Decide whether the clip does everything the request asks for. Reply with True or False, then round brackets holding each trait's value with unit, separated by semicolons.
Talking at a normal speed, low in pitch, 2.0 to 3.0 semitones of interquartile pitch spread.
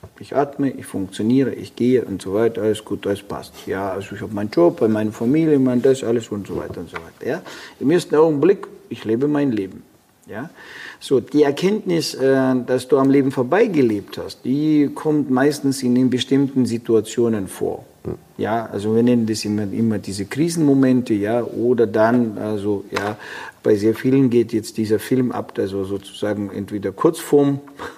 False (180 wpm; 120 Hz; 4.4 semitones)